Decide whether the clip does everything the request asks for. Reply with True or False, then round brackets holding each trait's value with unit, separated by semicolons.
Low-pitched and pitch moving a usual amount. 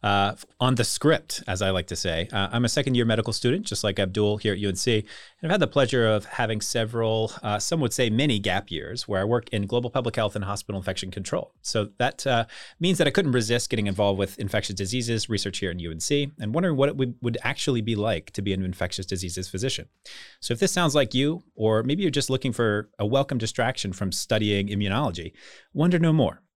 True (110 Hz; 4.4 semitones)